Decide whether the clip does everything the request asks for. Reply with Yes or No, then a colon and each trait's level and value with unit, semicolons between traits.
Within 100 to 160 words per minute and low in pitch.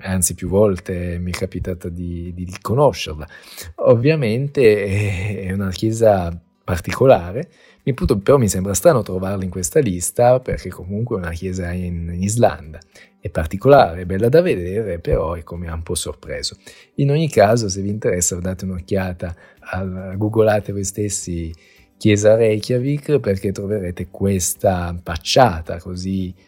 Yes: average, 140 wpm; very low, 95 Hz